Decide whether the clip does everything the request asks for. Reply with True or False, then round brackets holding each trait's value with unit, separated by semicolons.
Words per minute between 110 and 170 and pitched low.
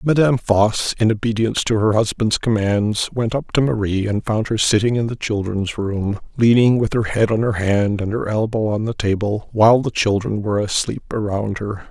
False (200 wpm; 110 Hz)